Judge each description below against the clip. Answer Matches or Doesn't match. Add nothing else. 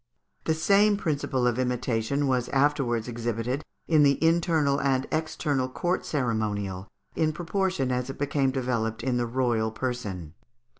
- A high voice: Doesn't match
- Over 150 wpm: Doesn't match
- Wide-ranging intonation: Doesn't match